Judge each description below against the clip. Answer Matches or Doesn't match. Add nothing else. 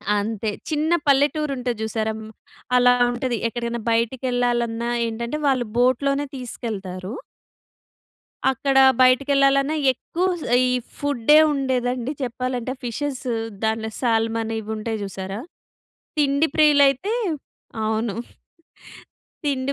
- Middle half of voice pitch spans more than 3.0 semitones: Matches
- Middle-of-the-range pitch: Doesn't match